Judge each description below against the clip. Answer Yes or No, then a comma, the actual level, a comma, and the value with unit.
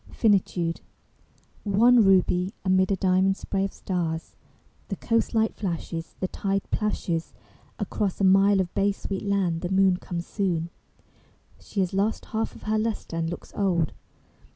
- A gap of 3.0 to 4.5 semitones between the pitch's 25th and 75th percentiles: No, narrow, 2.4 semitones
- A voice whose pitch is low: No, high, 190 Hz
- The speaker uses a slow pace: No, average, 155 wpm